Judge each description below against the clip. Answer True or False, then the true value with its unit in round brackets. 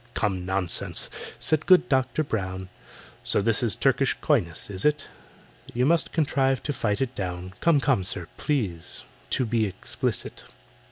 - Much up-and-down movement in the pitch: True (6.9 semitones)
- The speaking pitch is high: False (115 Hz)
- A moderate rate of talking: True (150 wpm)